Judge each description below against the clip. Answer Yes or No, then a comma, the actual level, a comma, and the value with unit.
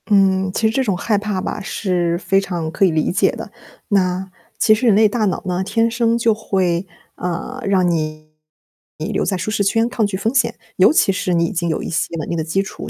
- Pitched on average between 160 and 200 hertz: Yes, high, 190 Hz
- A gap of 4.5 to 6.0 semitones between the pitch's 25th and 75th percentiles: No, average, 3.4 semitones